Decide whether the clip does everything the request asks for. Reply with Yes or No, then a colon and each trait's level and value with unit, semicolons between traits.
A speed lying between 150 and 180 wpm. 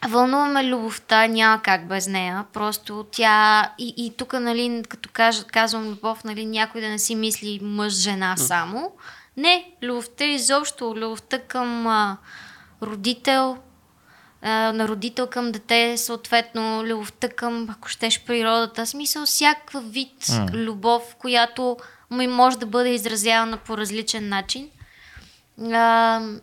No: average, 125 wpm